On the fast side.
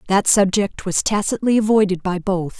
No: average, 160 wpm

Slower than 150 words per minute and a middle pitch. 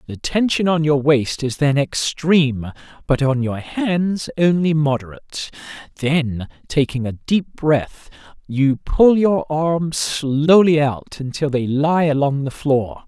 Yes: average, 140 wpm; medium, 145 Hz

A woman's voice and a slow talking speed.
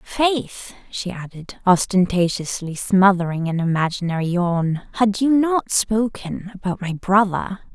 Yes: female; slow, 115 wpm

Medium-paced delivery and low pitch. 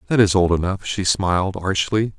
Yes: average, 190 wpm; very low, 95 Hz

